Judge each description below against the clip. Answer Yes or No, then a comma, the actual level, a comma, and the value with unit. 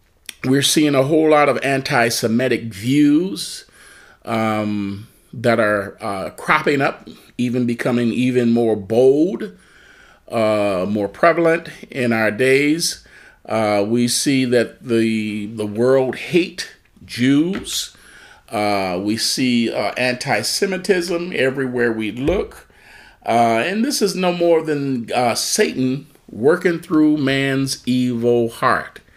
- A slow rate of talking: Yes, slow, 115 wpm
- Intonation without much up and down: No, average, 4.5 semitones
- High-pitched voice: No, low, 125 Hz